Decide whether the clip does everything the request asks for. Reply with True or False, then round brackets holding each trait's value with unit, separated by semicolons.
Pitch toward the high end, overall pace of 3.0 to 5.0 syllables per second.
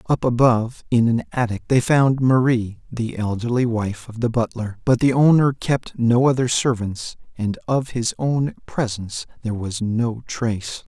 False (120 Hz; 4.6 syllables/s)